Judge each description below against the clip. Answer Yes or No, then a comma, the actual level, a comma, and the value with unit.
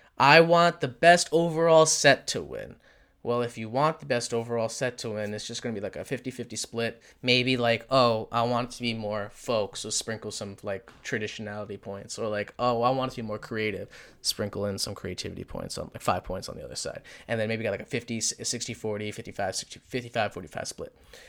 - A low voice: Yes, low, 115 Hz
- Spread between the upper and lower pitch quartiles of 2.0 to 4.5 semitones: Yes, average, 2.9 semitones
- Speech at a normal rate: No, fast, 210 wpm